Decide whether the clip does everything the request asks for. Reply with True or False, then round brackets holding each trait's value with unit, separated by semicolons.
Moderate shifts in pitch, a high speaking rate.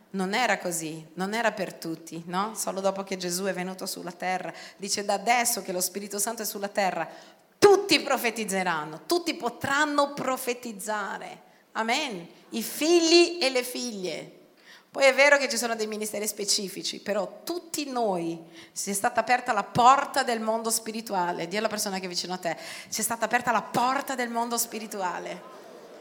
True (4.6 semitones; 175 wpm)